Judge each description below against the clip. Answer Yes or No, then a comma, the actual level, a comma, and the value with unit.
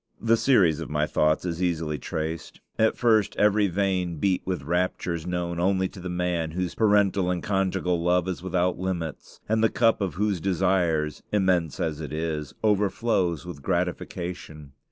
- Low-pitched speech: Yes, very low, 90 Hz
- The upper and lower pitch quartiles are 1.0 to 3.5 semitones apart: Yes, average, 2.8 semitones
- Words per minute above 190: No, average, 165 wpm